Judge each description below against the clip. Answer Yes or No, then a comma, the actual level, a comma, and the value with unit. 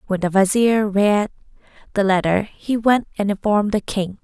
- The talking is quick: No, average, 170 wpm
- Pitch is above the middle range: Yes, high, 205 Hz